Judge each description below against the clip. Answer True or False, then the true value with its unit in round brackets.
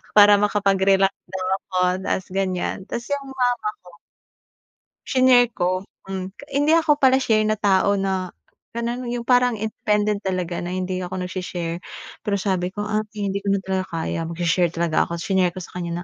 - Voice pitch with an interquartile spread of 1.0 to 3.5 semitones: True (2.8 semitones)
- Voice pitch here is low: False (195 Hz)